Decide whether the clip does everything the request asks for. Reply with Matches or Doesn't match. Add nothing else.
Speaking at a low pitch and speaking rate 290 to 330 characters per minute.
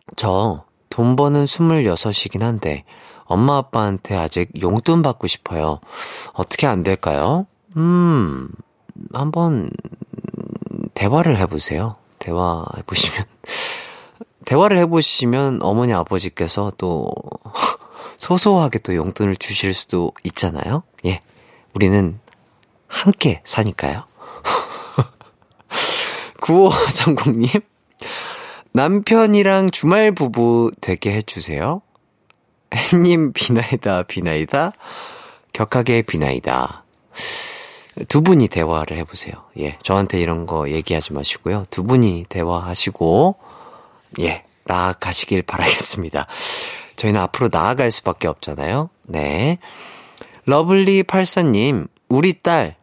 Doesn't match